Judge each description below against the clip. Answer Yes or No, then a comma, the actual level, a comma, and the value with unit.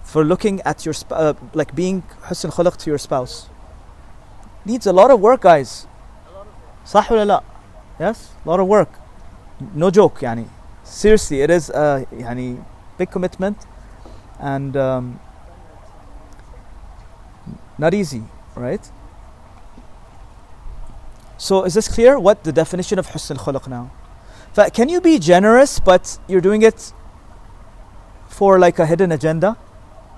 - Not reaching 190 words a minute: Yes, slow, 135 wpm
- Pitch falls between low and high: Yes, medium, 145 Hz